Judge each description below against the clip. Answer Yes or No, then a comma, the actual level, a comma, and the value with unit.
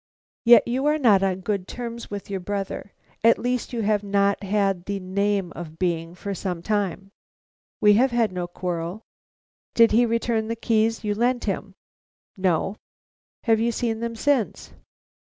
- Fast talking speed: No, average, 165 wpm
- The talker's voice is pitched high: Yes, high, 205 Hz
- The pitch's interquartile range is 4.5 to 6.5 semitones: No, average, 3.3 semitones